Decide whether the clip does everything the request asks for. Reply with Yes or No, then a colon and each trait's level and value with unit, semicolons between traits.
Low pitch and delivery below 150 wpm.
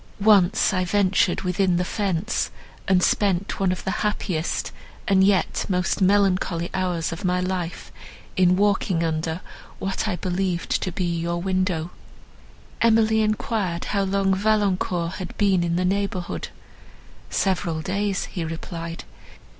No: medium, 185 Hz; slow, 135 wpm